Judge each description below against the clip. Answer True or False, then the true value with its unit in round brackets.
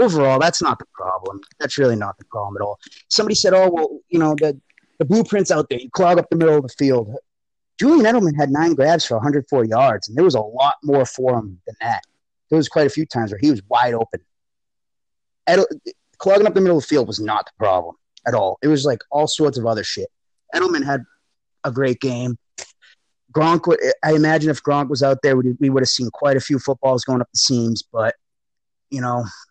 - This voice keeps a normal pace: False (220 wpm)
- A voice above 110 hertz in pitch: True (140 Hz)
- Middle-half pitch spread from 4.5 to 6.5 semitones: True (4.8 semitones)